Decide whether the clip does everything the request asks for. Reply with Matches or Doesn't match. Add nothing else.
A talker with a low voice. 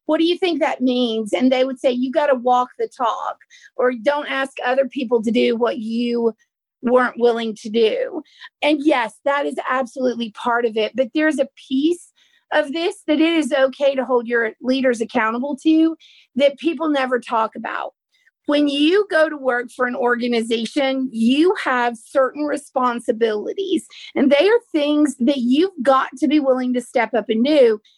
Doesn't match